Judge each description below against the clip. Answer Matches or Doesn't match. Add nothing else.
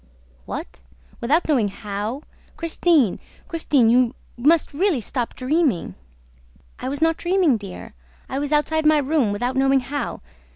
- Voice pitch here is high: Matches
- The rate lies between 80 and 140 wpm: Matches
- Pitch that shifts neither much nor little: Matches